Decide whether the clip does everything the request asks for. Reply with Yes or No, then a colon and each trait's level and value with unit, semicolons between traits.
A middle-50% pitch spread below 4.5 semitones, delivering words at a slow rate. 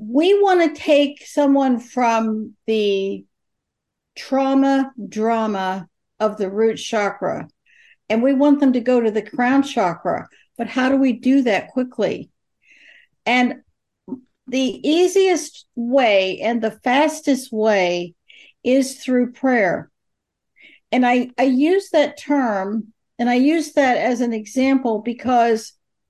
Yes: average, 3.7 semitones; slow, 125 wpm